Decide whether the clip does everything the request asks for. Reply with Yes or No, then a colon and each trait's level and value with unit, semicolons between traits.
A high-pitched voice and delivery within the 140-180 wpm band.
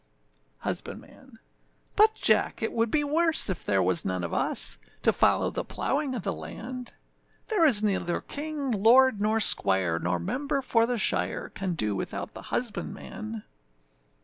Yes: high, 225 Hz; average, 155 wpm